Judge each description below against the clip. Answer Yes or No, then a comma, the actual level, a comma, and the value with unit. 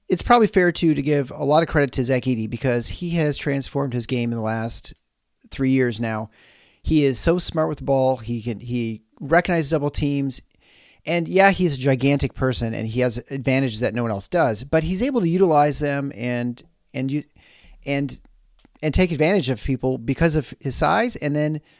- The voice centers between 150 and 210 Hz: No, medium, 140 Hz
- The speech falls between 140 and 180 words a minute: No, fast, 205 wpm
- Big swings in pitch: No, average, 4.3 semitones